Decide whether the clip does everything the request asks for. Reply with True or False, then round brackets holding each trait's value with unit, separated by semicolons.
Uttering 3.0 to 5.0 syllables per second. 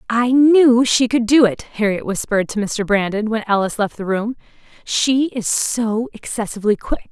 True (4.9 syllables/s)